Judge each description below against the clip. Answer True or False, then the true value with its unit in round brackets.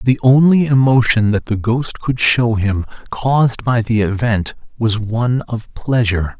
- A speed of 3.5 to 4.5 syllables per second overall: True (4.3 syllables/s)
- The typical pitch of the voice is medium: False (115 Hz)